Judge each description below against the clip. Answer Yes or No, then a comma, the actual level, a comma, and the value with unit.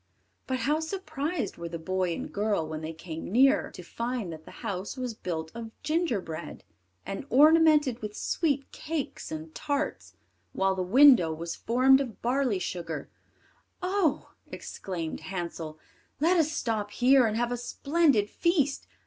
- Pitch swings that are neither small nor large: No, wide, 8.2 semitones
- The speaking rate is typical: Yes, average, 150 wpm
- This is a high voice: Yes, high, 235 Hz